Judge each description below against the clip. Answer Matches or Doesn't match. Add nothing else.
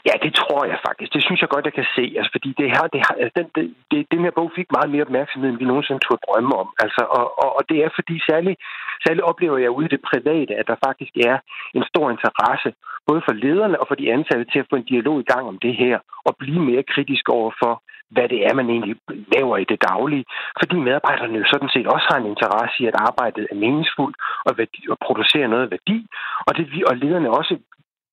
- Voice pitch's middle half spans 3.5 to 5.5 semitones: Matches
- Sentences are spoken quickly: Matches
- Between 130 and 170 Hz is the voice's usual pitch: Matches